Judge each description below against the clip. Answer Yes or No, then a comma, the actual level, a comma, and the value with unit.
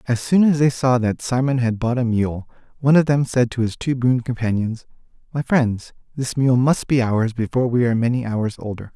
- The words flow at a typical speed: No, fast, 220 wpm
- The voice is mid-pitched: No, low, 125 Hz